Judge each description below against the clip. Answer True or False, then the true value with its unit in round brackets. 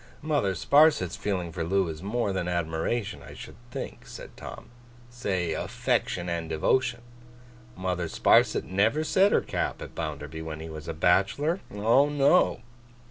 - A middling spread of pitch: False (6.8 semitones)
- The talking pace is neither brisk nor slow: True (150 wpm)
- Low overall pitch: True (95 Hz)